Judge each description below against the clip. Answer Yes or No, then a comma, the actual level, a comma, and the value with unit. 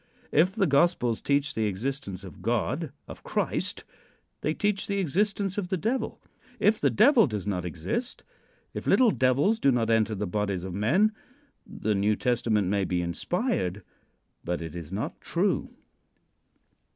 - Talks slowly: No, average, 155 wpm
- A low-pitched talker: Yes, low, 125 Hz